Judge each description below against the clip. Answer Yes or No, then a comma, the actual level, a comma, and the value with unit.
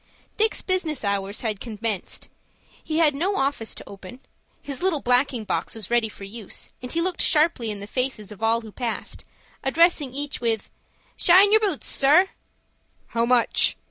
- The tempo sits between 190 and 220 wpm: No, average, 170 wpm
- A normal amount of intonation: No, wide, 6.4 semitones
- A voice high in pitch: Yes, very high, 250 Hz